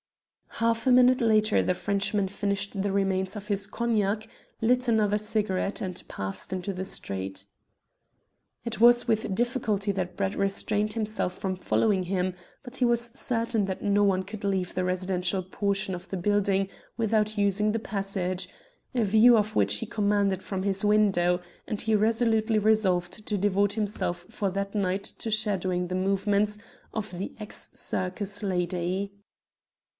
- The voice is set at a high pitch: Yes, high, 200 Hz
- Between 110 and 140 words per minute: No, average, 155 wpm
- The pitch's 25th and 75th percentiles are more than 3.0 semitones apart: No, narrow, 2.4 semitones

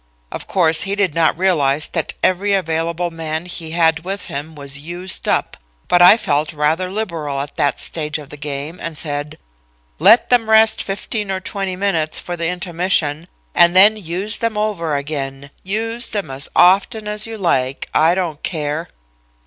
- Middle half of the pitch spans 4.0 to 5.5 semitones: Yes, average, 4.4 semitones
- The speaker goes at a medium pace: Yes, average, 175 wpm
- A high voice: No, medium, 170 Hz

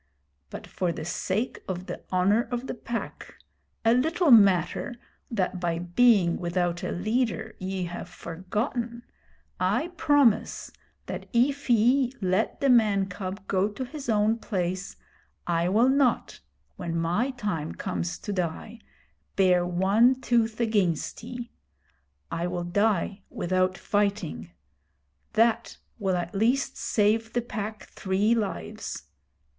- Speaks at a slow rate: Yes, slow, 130 wpm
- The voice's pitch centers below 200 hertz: No, high, 205 Hz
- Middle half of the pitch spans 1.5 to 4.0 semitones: No, average, 4.7 semitones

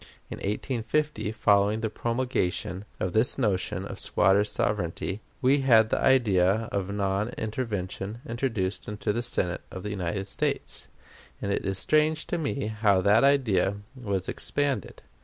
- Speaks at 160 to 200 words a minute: No, average, 145 wpm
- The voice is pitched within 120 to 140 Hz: No, low, 105 Hz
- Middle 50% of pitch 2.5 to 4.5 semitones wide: Yes, average, 3.6 semitones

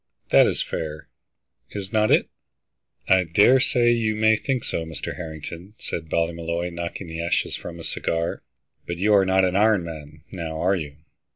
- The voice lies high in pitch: No, very low, 85 Hz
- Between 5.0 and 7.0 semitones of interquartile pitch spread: No, average, 3.9 semitones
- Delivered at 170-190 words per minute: Yes, average, 175 wpm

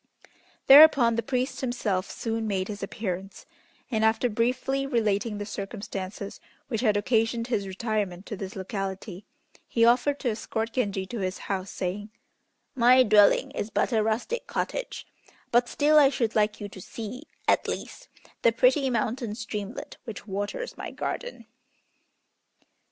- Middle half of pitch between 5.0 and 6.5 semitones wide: No, average, 3.5 semitones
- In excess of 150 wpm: No, average, 145 wpm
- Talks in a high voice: Yes, high, 220 Hz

